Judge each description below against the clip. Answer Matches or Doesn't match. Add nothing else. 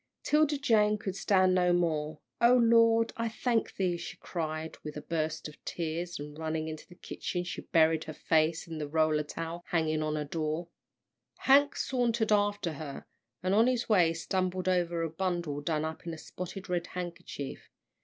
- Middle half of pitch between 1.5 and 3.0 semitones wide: Doesn't match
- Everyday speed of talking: Matches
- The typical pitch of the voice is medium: Matches